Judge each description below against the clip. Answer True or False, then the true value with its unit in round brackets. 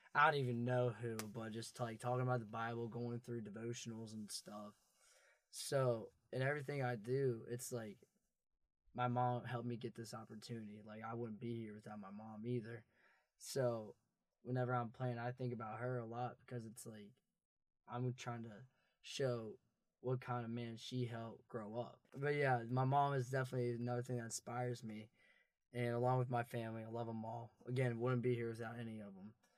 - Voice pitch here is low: True (120 Hz)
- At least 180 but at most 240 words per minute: True (190 wpm)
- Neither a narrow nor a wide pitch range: False (1.6 semitones)